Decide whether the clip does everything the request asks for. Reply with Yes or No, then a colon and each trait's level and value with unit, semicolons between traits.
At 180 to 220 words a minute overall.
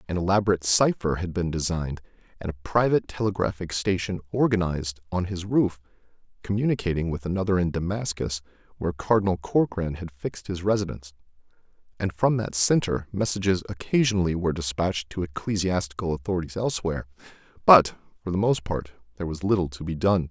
No: average, 150 wpm